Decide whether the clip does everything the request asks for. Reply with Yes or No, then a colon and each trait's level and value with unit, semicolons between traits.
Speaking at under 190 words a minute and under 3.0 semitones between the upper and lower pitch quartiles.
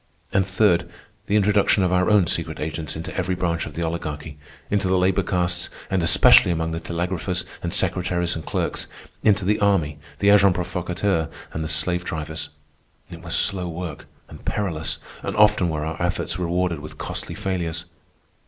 Yes: average, 170 wpm; narrow, 2.6 semitones